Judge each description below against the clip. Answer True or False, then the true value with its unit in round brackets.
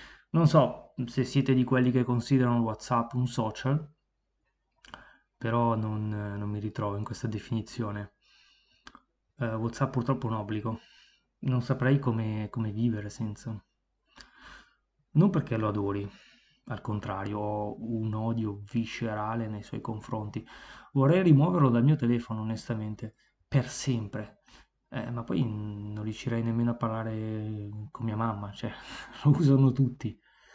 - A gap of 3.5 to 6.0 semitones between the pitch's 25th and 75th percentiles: False (3.0 semitones)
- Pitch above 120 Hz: False (115 Hz)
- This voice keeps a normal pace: True (130 wpm)